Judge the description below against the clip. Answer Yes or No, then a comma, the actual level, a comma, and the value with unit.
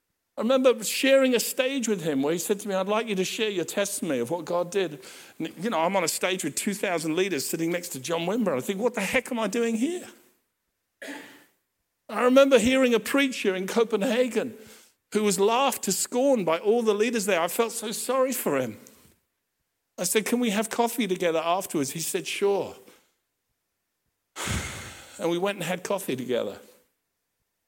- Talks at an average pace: Yes, average, 190 wpm